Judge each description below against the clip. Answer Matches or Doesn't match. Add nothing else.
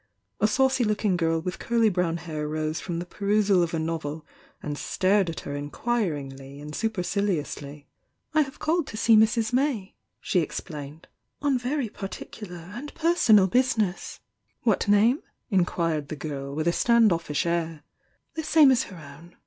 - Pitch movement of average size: Doesn't match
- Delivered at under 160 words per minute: Doesn't match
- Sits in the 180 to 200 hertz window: Matches